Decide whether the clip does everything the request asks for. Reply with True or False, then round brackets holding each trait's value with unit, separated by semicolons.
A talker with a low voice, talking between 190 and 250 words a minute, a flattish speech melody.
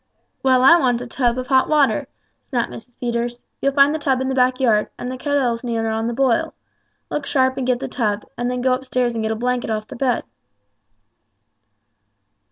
False (250 Hz; 200 wpm; 2.0 semitones)